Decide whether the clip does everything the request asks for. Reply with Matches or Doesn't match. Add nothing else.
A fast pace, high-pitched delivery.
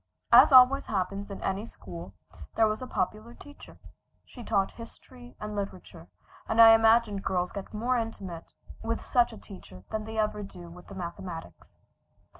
Doesn't match